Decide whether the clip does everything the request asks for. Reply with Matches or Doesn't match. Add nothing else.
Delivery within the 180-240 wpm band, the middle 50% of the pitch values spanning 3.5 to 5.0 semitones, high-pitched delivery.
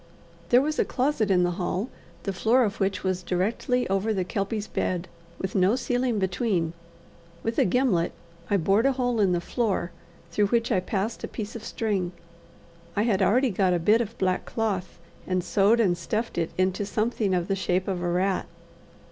Matches